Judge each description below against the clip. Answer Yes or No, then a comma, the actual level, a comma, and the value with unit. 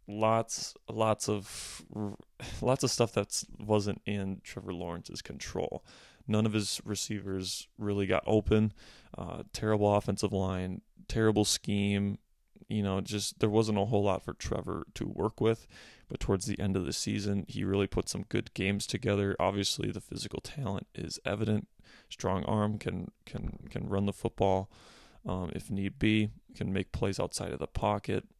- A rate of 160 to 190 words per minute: Yes, average, 165 wpm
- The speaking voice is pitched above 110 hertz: No, low, 100 Hz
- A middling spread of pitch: No, narrow, 1.9 semitones